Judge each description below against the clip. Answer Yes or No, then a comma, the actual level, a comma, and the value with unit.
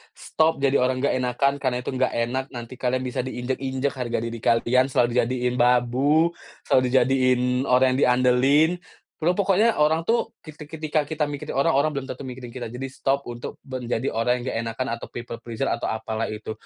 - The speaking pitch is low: Yes, low, 130 Hz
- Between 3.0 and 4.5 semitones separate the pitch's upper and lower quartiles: No, narrow, 2.4 semitones